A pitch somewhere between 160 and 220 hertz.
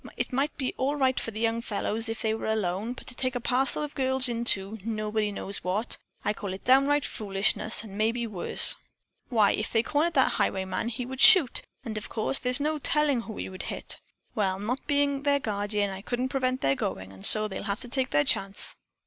No: high, 230 Hz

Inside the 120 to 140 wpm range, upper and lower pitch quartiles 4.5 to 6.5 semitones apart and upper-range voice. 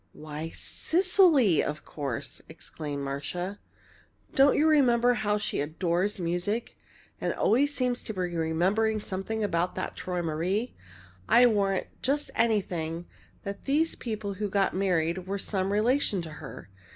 Yes: slow, 135 wpm; wide, 5.6 semitones; high, 195 Hz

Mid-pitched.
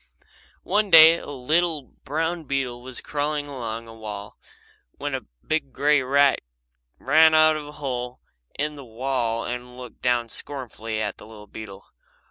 No: low, 130 Hz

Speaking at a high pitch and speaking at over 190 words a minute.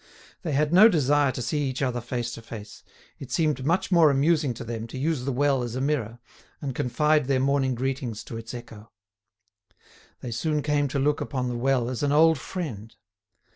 No: low, 135 Hz; average, 200 wpm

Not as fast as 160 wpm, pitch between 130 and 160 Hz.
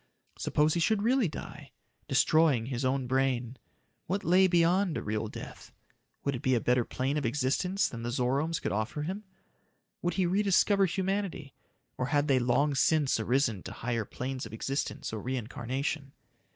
No: average, 165 wpm; medium, 140 Hz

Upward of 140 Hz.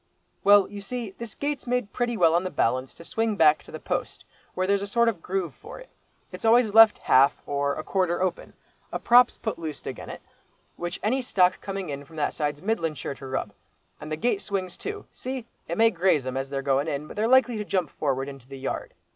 Yes: medium, 185 Hz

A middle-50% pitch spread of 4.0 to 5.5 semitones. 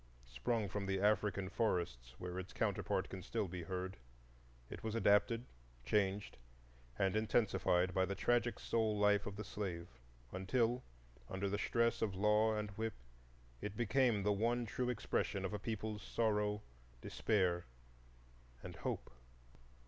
No: average, 2.8 semitones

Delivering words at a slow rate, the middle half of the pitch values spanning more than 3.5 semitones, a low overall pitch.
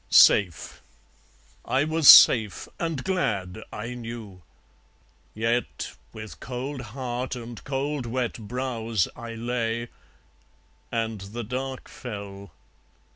No: slow, 100 wpm; average, 2.9 semitones; low, 120 Hz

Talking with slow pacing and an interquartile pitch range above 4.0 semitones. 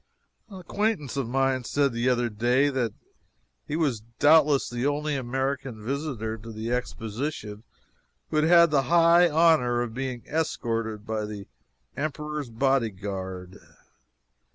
Yes: slow, 130 wpm; average, 4.9 semitones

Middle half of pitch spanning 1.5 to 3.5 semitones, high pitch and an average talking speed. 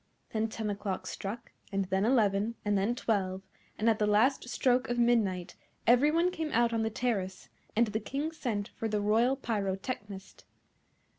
Yes: average, 3.1 semitones; high, 220 Hz; average, 170 wpm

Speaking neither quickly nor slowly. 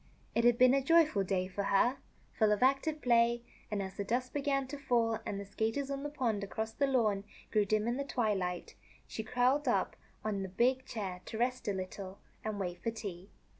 No: fast, 210 wpm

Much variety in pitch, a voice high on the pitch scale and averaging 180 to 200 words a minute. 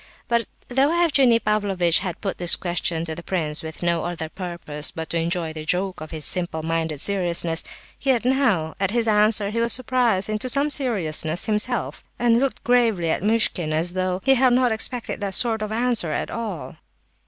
Yes: wide, 5.9 semitones; high, 195 Hz; average, 190 wpm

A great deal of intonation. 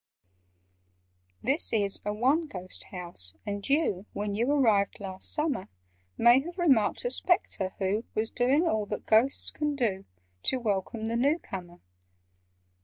Yes: wide, 5.8 semitones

